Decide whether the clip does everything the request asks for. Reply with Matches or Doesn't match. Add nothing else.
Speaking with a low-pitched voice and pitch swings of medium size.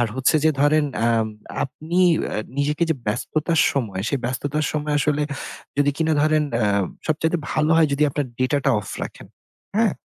Doesn't match